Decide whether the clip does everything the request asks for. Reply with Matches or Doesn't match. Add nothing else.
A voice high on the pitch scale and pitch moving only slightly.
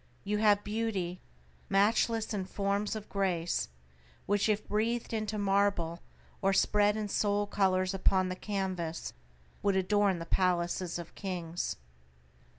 Matches